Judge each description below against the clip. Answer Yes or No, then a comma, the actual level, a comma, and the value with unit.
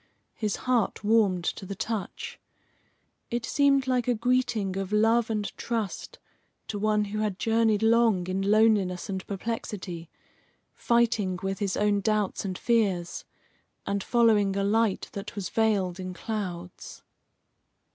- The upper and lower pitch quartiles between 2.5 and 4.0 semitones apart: Yes, average, 2.8 semitones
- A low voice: No, high, 210 Hz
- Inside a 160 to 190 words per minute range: No, slow, 135 wpm